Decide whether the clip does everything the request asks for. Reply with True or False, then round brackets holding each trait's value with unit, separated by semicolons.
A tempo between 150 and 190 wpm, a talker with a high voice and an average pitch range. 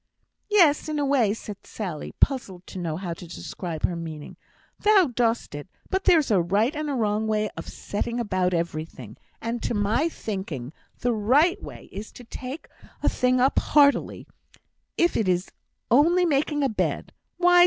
False (175 wpm; 225 Hz; 7.7 semitones)